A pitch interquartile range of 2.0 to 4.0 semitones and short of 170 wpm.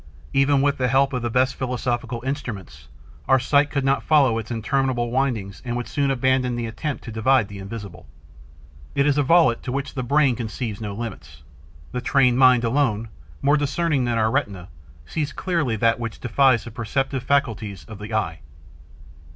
No: average, 3.5 semitones; average, 180 wpm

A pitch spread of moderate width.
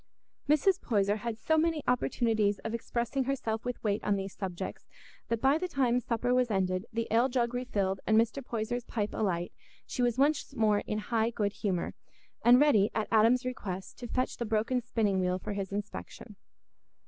Yes: average, 3.3 semitones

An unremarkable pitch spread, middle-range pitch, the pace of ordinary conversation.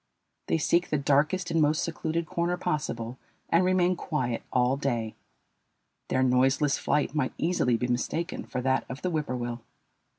Yes: average, 4.8 semitones; medium, 145 Hz; average, 155 wpm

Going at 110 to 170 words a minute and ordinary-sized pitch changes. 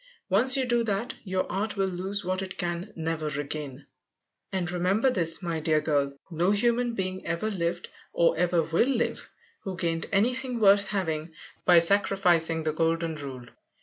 Yes: average, 165 wpm; average, 3.6 semitones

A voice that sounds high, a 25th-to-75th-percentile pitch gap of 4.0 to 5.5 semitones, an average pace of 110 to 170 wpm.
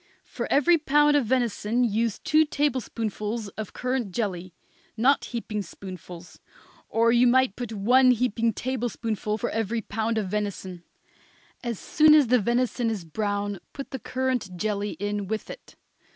No: high, 225 Hz; average, 3.6 semitones; average, 150 wpm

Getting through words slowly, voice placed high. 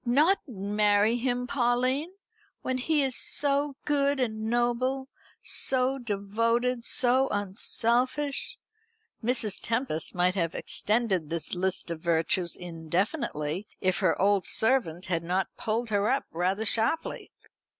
Yes: slow, 120 wpm; high, 230 Hz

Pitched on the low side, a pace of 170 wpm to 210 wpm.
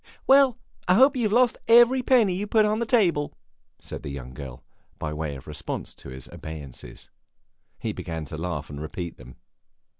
Yes: very low, 90 Hz; average, 185 wpm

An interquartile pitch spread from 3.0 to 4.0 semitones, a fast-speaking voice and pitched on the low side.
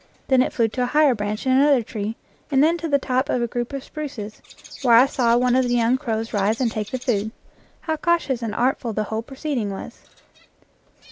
No: average, 3.4 semitones; fast, 220 wpm; high, 245 Hz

